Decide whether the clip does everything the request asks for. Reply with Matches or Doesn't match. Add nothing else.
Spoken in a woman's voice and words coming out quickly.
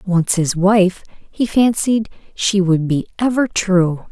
Doesn't match